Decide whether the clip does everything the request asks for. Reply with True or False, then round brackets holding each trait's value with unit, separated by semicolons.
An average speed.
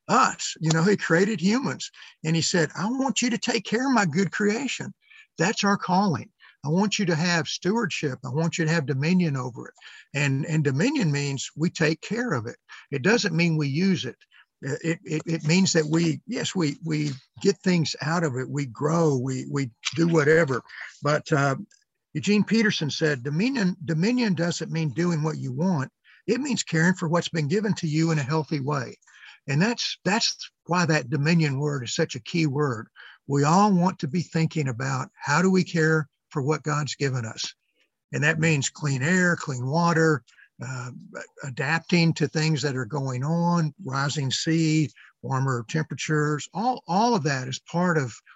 True (185 wpm)